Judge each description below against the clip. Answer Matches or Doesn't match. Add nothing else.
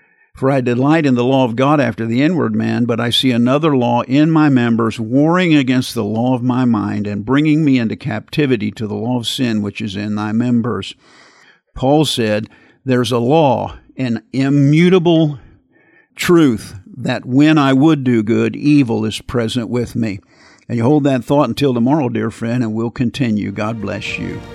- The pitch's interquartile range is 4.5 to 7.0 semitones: Doesn't match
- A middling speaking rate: Matches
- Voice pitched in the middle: Doesn't match